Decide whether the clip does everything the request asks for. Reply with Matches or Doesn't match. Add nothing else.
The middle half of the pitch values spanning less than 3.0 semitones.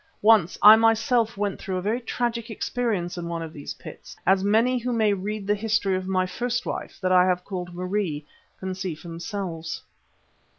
Doesn't match